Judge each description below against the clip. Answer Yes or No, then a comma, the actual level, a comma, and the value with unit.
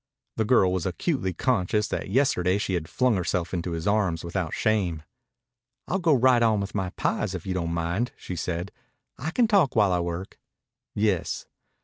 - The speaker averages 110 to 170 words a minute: No, average, 180 wpm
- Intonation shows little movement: No, average, 4.4 semitones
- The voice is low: Yes, very low, 95 Hz